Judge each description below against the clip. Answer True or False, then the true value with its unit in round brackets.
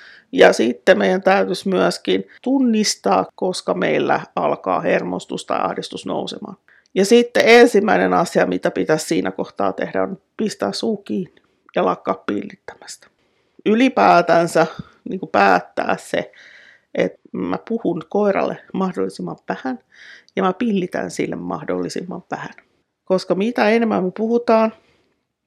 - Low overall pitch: False (195 Hz)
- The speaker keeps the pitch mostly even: False (3.8 semitones)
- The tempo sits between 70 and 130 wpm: True (120 wpm)